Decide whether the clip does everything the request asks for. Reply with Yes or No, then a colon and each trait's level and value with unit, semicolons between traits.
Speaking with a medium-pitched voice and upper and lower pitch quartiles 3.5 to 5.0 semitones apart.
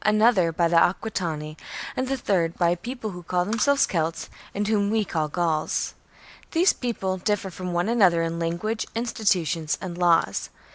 Yes: medium, 180 Hz; average, 4.4 semitones